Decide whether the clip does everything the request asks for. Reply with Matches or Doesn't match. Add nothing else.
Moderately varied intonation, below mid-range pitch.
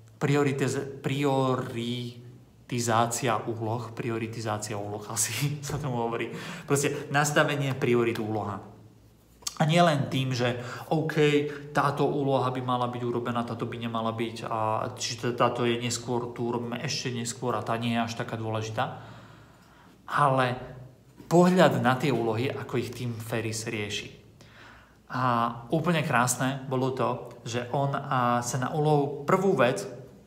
Matches